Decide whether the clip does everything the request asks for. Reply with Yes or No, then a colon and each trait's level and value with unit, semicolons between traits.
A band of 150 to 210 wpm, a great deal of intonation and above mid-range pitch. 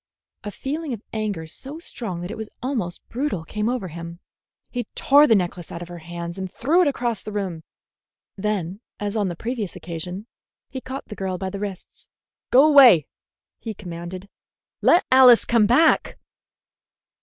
Yes: average, 170 wpm; wide, 5.9 semitones; high, 210 Hz